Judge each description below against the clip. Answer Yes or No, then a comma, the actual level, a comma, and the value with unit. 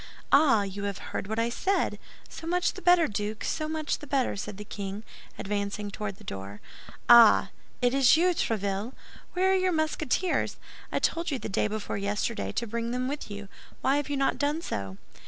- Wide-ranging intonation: Yes, wide, 7.2 semitones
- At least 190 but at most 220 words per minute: Yes, average, 195 wpm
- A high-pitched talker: Yes, high, 235 Hz